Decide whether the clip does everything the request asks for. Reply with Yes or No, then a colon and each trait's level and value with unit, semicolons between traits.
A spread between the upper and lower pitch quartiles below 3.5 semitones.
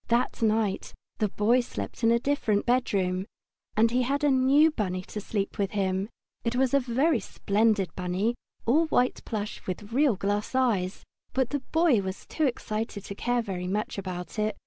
No: average, 4.2 semitones